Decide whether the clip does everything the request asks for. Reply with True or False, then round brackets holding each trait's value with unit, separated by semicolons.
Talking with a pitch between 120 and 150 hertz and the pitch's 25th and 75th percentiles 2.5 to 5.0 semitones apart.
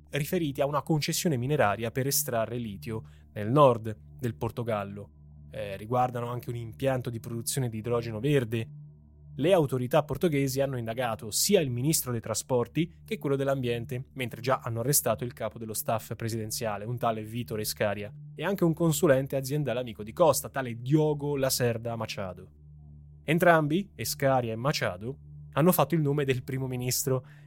True (125 Hz; 4.2 semitones)